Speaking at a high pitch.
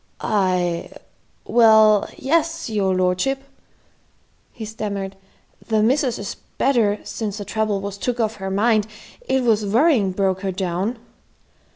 Yes: high, 210 Hz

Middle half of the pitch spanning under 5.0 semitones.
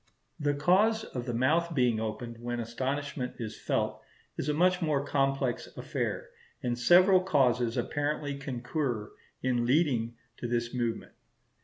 Yes: average, 3.9 semitones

